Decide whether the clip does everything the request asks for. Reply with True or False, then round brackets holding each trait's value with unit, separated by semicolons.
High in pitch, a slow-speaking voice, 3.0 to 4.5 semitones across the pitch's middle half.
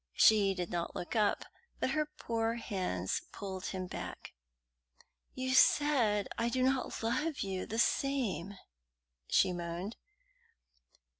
False (215 Hz; 125 wpm; 5.6 semitones)